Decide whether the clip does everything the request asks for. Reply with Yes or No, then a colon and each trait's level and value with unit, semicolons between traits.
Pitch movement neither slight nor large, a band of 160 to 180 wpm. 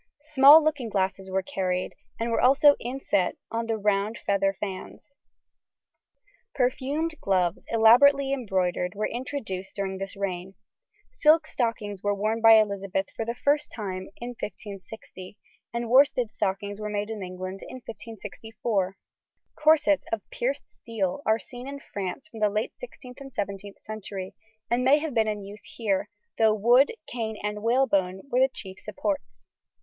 No: average, 4.3 semitones; average, 150 wpm